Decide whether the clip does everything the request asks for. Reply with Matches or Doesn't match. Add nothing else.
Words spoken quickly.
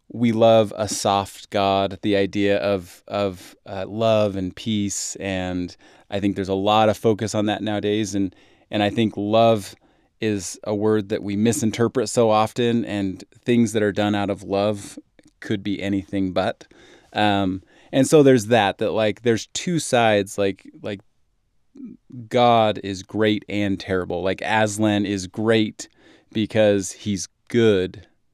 Doesn't match